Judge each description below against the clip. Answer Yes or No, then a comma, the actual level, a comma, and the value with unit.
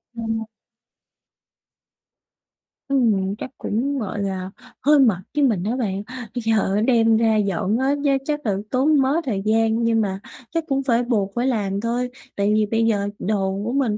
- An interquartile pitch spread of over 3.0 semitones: Yes, average, 3.8 semitones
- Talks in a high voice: Yes, high, 225 Hz